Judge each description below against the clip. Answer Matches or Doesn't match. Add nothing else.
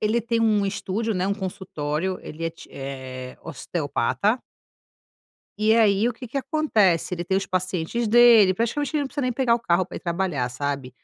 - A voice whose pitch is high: Matches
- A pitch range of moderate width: Doesn't match